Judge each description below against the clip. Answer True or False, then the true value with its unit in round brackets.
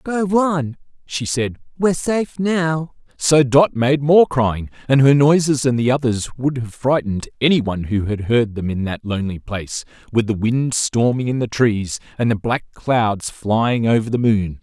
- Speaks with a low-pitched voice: True (125 Hz)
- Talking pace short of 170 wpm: False (185 wpm)